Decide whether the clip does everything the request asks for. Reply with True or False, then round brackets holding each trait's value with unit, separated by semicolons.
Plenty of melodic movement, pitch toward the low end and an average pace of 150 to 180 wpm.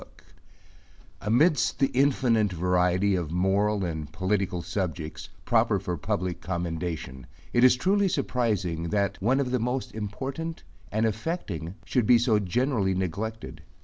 False (5.7 semitones; 100 Hz; 135 wpm)